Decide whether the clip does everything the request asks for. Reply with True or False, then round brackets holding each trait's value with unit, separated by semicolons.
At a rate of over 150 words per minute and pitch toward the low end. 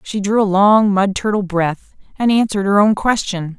False (200 wpm; 200 Hz)